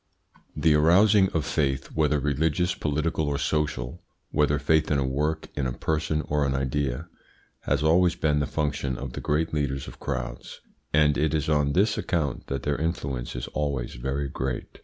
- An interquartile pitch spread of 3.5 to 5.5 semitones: No, narrow, 2.4 semitones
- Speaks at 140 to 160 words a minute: No, average, 180 wpm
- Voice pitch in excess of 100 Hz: No, very low, 75 Hz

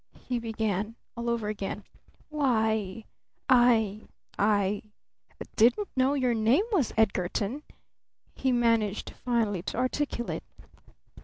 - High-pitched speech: Yes, high, 225 Hz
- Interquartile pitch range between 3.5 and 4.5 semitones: No, average, 3.0 semitones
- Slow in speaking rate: Yes, slow, 100 wpm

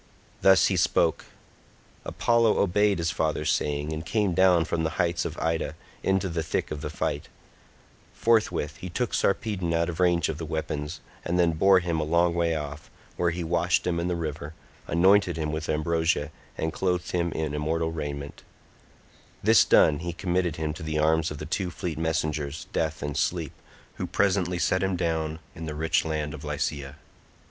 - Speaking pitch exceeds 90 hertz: No, very low, 80 Hz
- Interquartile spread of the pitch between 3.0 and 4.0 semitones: No, narrow, 2.4 semitones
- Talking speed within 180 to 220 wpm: Yes, average, 185 wpm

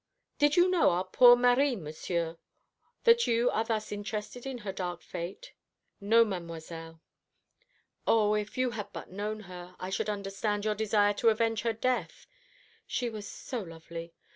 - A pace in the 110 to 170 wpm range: Yes, average, 160 wpm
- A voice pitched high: Yes, high, 210 Hz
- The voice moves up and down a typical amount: Yes, average, 4.3 semitones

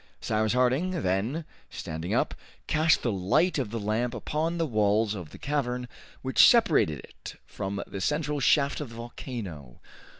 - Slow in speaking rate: No, average, 160 wpm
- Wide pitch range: Yes, wide, 6.6 semitones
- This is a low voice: Yes, low, 120 Hz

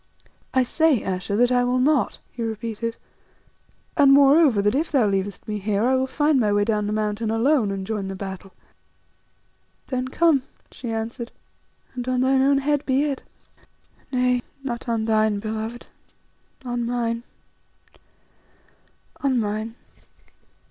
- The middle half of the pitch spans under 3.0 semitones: No, average, 3.6 semitones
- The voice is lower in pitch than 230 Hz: No, high, 235 Hz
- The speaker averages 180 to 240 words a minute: No, average, 140 wpm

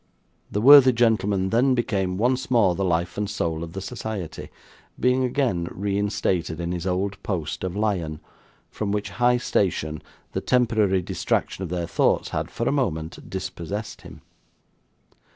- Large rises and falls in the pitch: No, average, 4.4 semitones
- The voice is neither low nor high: No, low, 100 Hz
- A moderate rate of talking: Yes, average, 150 wpm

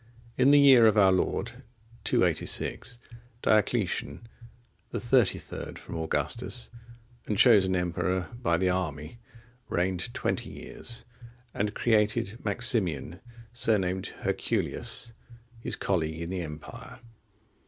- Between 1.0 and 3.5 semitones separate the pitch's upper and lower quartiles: No, average, 4.7 semitones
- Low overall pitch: Yes, very low, 95 Hz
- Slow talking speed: Yes, slow, 110 wpm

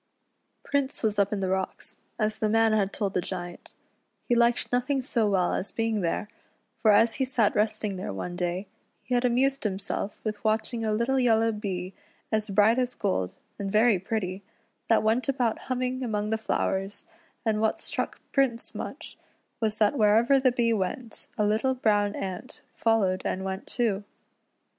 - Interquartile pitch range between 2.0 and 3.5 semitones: Yes, average, 3.2 semitones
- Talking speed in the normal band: Yes, average, 175 wpm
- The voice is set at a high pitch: Yes, high, 215 Hz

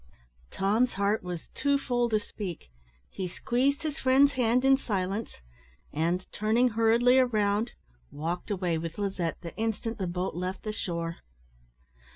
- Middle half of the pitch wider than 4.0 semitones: Yes, average, 5.1 semitones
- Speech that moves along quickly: No, average, 145 wpm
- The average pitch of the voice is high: Yes, high, 210 Hz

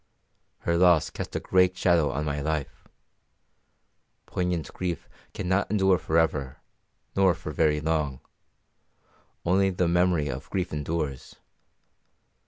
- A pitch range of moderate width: Yes, average, 3.3 semitones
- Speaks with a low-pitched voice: Yes, very low, 85 Hz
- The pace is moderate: No, slow, 120 wpm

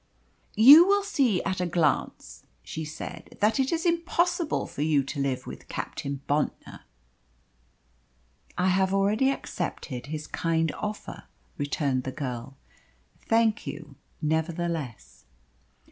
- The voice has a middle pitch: Yes, medium, 165 Hz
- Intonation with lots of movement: Yes, wide, 7.6 semitones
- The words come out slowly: Yes, slow, 120 wpm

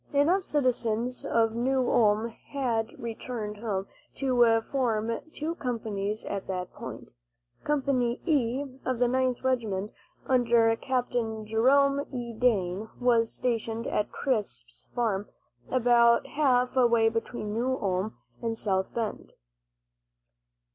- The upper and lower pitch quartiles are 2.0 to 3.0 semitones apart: Yes, average, 2.7 semitones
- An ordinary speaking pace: No, slow, 115 wpm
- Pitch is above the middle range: Yes, high, 235 Hz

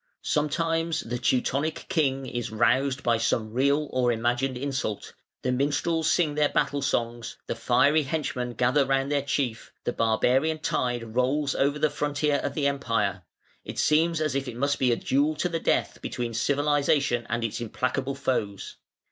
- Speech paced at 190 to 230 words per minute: No, average, 165 wpm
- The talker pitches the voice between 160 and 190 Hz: No, low, 135 Hz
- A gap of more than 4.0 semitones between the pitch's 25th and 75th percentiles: No, average, 3.4 semitones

